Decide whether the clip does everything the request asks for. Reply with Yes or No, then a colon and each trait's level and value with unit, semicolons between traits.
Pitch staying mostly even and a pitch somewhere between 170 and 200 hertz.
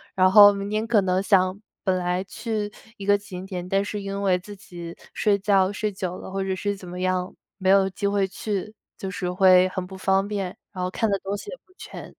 Yes: narrow, 1.6 semitones; high, 195 Hz